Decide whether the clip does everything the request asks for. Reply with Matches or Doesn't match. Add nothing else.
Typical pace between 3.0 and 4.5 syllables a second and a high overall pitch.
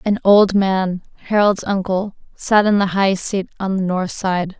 Matches